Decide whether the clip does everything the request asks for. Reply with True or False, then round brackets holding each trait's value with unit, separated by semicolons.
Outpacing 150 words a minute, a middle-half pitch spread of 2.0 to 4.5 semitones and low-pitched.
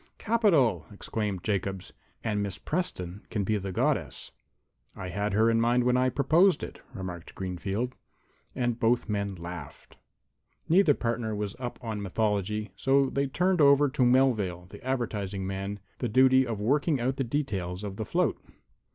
False (160 wpm; 5.1 semitones; 110 Hz)